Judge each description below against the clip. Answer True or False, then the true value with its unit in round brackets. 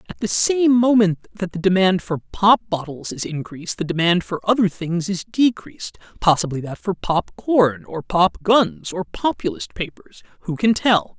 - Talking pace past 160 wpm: True (170 wpm)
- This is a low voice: False (180 Hz)